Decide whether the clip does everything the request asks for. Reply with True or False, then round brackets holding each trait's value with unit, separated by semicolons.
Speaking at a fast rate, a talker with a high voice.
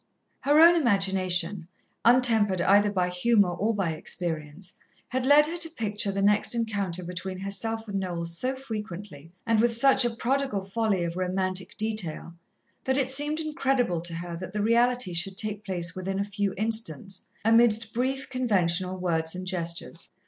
False (165 wpm; 200 Hz)